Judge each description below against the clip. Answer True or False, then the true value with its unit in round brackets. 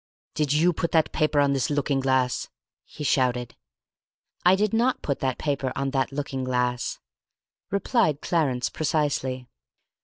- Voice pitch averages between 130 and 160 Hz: True (140 Hz)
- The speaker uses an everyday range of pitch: True (3.3 semitones)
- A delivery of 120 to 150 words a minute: True (145 wpm)